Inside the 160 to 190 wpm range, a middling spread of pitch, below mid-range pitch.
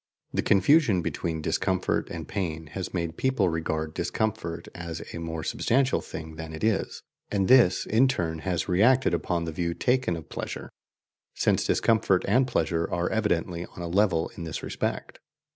Yes: average, 165 wpm; average, 4.7 semitones; very low, 90 Hz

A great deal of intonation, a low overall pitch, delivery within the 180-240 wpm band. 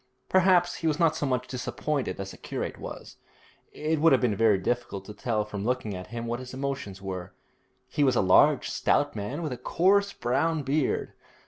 Yes: wide, 6.2 semitones; low, 125 Hz; average, 200 wpm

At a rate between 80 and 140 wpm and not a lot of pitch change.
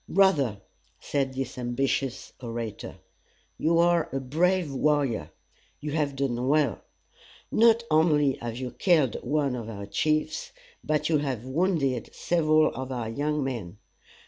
No: slow, 135 wpm; average, 3.7 semitones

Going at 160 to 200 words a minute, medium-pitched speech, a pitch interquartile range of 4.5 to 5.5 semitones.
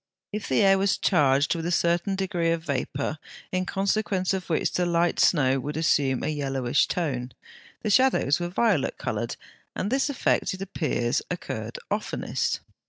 Yes: average, 165 wpm; medium, 170 Hz; average, 5.2 semitones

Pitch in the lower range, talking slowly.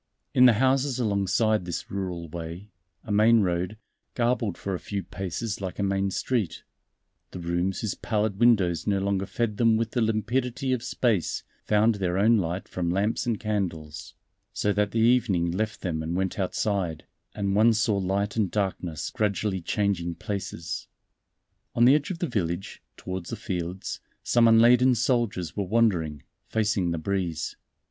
No: low, 100 Hz; average, 165 wpm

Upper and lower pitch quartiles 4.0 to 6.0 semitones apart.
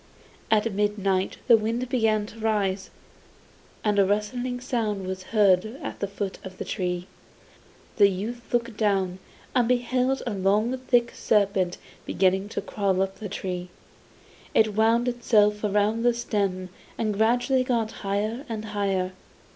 No: average, 3.2 semitones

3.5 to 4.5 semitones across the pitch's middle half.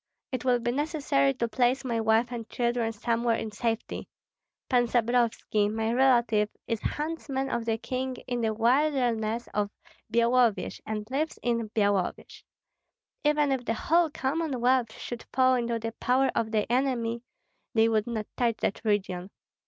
No: narrow, 2.5 semitones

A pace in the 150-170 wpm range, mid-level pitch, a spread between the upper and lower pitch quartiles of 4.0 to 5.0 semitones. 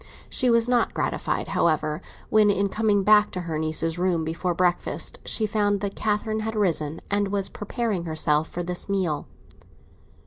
No: average, 165 wpm; high, 195 Hz; average, 4.3 semitones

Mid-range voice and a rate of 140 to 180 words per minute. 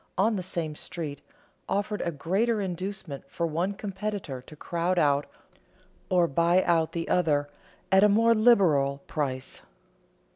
Yes: medium, 175 Hz; average, 145 wpm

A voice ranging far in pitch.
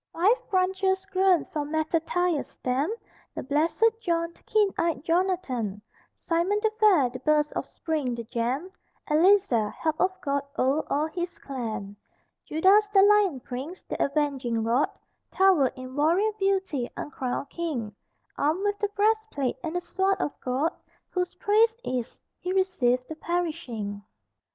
Yes: wide, 6.3 semitones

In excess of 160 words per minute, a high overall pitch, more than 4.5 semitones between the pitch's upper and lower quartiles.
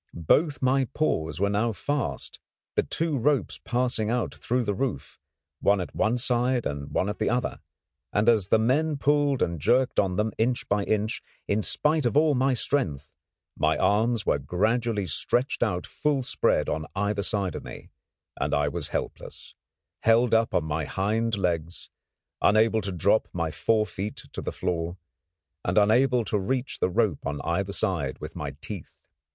No: average, 175 wpm; low, 110 Hz; average, 5.0 semitones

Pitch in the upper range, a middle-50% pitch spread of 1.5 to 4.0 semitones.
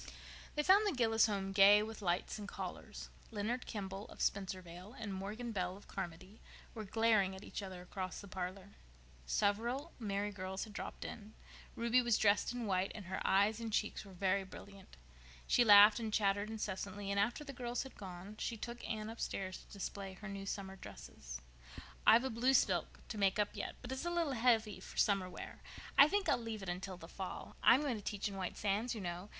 Yes: high, 205 Hz; average, 3.0 semitones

